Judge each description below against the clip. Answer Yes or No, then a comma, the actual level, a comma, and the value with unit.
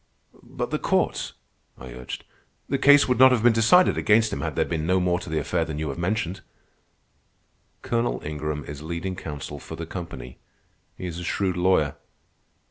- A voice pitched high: No, very low, 85 Hz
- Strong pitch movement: Yes, wide, 6.0 semitones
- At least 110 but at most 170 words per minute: No, average, 185 wpm